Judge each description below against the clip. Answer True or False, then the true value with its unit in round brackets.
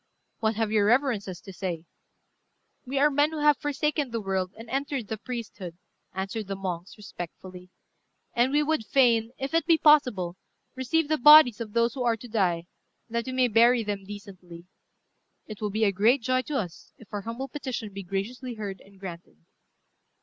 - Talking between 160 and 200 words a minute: True (185 wpm)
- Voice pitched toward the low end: False (225 Hz)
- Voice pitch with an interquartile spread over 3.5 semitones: True (5.0 semitones)